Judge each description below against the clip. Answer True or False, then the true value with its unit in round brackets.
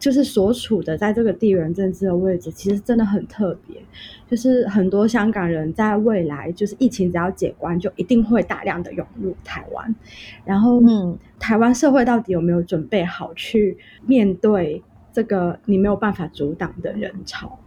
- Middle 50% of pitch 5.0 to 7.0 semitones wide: False (4.2 semitones)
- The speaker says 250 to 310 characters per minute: True (275 characters per minute)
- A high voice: True (200 Hz)